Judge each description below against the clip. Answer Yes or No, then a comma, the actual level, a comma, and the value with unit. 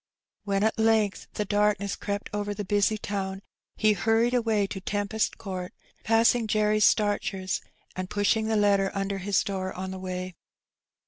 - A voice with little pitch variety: Yes, narrow, 1.8 semitones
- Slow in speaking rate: No, average, 155 wpm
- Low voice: No, high, 205 Hz